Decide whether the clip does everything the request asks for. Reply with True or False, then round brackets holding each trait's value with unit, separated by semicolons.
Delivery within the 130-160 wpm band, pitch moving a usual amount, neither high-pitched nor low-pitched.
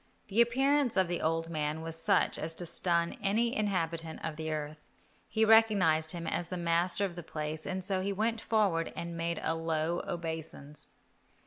False (185 wpm; 3.6 semitones; 170 Hz)